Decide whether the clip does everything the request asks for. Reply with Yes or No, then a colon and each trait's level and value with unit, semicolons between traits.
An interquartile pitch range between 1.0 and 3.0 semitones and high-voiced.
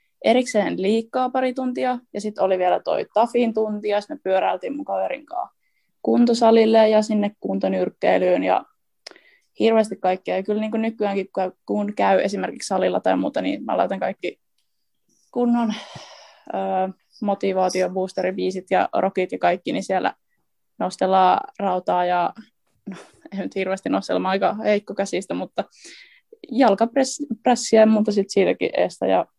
No: average, 4.0 semitones; high, 210 Hz